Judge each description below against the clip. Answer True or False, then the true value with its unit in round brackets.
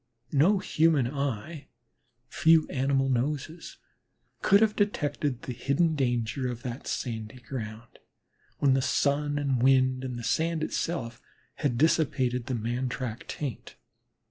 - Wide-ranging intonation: False (3.5 semitones)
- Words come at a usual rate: False (130 wpm)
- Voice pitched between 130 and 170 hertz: True (135 Hz)